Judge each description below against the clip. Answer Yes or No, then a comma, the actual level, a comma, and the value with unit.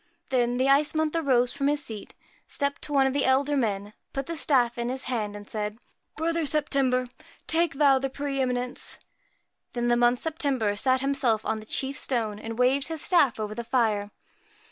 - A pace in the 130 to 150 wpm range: No, average, 195 wpm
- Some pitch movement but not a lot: Yes, average, 3.1 semitones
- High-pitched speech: Yes, very high, 260 Hz